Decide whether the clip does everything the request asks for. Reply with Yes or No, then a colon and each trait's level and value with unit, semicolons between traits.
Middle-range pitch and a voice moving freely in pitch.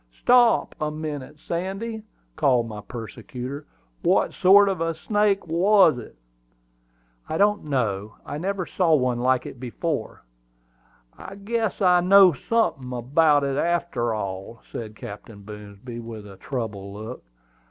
Yes: medium, 145 Hz; wide, 8.0 semitones